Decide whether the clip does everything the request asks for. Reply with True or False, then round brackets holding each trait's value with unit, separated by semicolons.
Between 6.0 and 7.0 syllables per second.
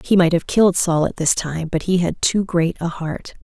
False (5.0 syllables/s)